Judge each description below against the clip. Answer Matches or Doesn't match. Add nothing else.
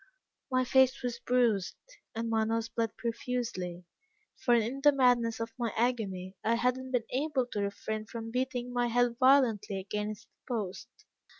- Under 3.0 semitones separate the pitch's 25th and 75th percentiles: Matches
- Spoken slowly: Doesn't match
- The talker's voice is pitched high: Matches